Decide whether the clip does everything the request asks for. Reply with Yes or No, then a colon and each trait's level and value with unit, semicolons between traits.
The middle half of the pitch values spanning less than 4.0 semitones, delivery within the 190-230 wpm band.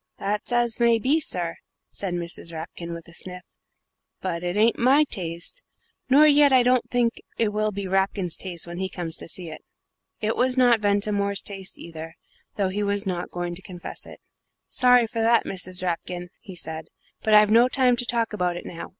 No: average, 4.9 semitones; average, 195 wpm